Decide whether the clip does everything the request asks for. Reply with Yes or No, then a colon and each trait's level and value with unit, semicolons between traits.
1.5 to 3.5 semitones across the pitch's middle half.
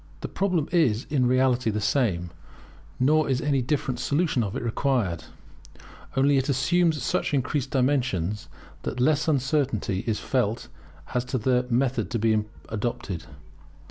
No: average, 4.0 semitones